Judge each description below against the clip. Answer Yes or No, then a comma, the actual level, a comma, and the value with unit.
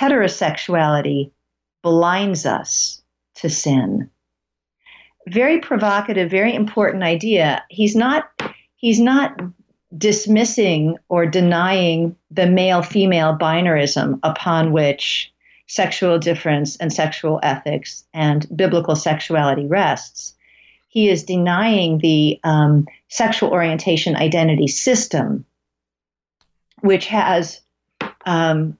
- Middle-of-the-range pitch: Yes, medium, 170 Hz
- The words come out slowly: Yes, slow, 90 wpm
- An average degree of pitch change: Yes, average, 4.0 semitones